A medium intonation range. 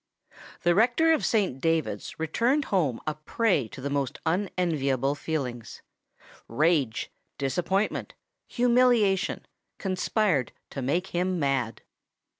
No: wide, 6.5 semitones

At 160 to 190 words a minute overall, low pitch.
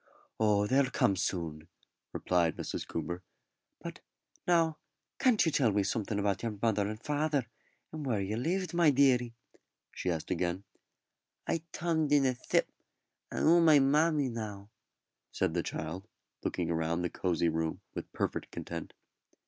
No: average, 150 wpm; low, 110 Hz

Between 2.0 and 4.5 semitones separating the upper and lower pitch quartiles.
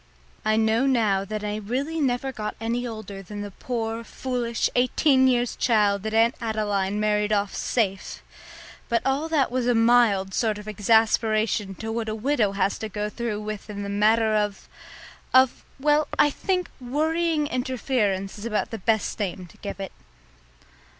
Yes: average, 3.1 semitones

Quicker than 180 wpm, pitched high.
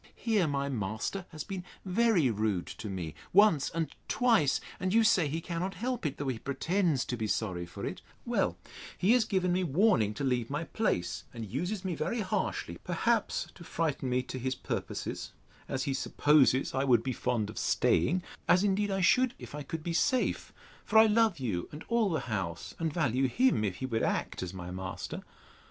No: average, 200 wpm; medium, 155 Hz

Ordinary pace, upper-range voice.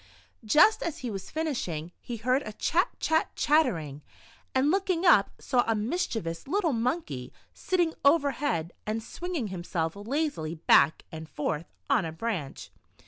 Yes: average, 145 wpm; high, 230 Hz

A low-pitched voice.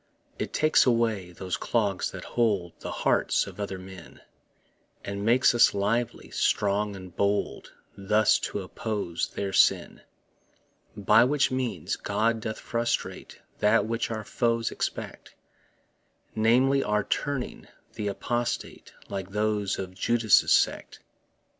Yes: low, 105 Hz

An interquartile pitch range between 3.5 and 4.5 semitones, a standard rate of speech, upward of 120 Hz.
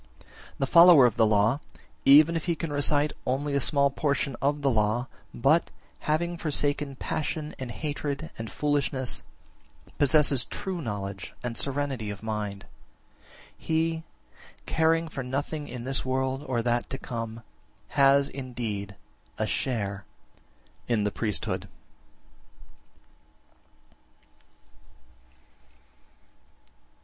No: average, 4.1 semitones; slow, 115 wpm; low, 135 Hz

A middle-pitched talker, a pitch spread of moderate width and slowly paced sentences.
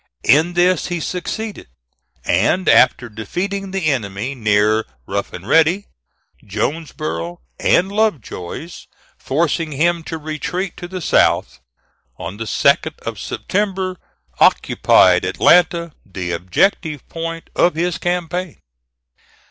No: medium, 160 Hz; wide, 8.7 semitones; slow, 110 wpm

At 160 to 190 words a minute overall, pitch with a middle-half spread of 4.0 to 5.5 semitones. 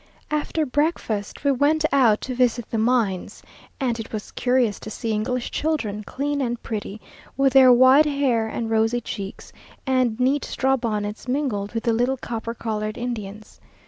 No: average, 165 wpm; average, 3.4 semitones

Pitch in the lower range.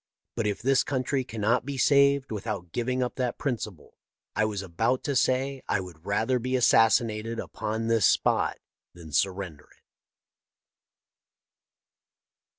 Yes: low, 115 Hz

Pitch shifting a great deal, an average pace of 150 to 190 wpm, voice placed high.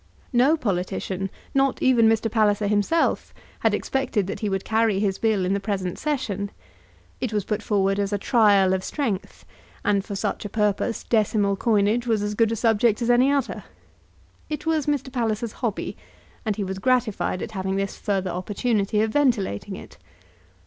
No: average, 3.3 semitones; average, 175 wpm; high, 210 Hz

